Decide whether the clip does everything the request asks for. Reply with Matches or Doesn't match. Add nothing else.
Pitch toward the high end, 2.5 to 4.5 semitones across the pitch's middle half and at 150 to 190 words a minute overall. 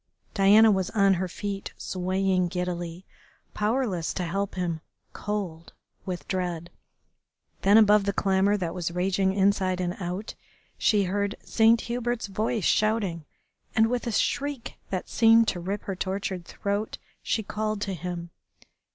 Doesn't match